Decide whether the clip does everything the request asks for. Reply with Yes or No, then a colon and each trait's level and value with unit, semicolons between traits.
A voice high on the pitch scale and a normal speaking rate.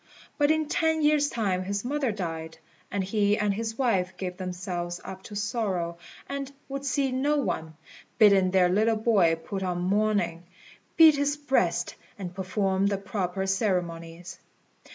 Yes: high, 200 Hz; average, 155 wpm